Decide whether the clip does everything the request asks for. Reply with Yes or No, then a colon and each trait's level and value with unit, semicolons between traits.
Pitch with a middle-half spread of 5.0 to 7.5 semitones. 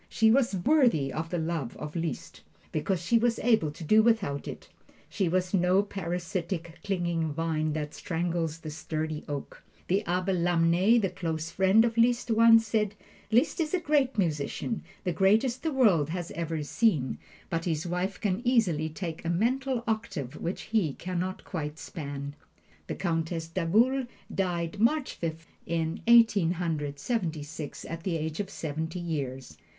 Yes: average, 5.3 semitones